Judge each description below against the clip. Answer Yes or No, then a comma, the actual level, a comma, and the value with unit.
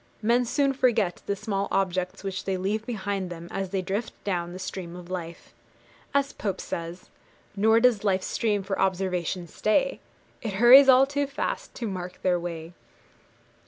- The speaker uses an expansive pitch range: No, average, 4.0 semitones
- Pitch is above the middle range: Yes, high, 195 Hz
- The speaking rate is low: No, average, 165 wpm